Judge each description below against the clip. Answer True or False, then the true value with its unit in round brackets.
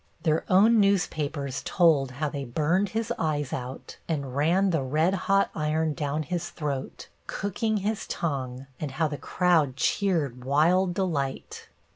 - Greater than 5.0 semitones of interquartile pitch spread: False (4.7 semitones)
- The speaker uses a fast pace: False (145 wpm)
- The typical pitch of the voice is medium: True (155 Hz)